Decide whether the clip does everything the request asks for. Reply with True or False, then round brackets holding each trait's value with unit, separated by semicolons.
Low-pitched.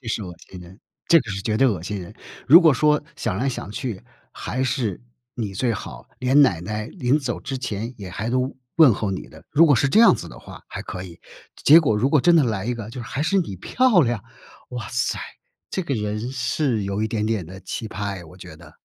True (115 Hz)